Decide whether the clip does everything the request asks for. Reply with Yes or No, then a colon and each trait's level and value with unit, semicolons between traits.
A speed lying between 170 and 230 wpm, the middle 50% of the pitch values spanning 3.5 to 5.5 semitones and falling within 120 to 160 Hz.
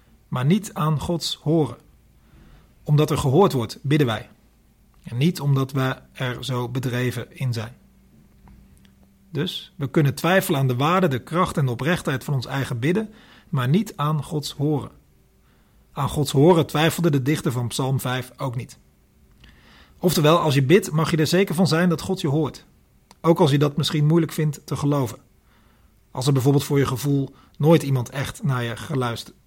Yes: average, 175 wpm; average, 4.6 semitones; medium, 140 Hz